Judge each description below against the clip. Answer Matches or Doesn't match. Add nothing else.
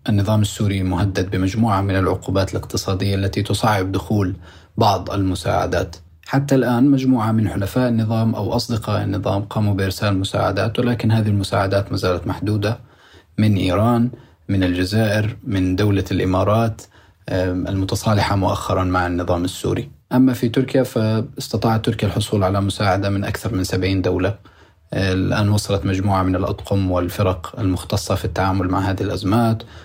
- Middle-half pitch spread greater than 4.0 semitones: Doesn't match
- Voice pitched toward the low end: Matches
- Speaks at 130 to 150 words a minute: Matches